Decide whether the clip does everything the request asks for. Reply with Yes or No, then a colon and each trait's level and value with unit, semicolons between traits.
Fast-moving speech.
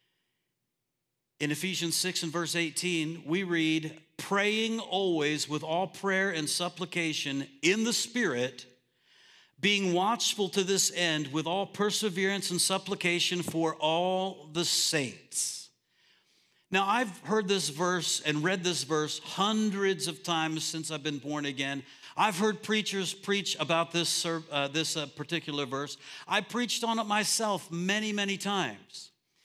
No: average, 140 wpm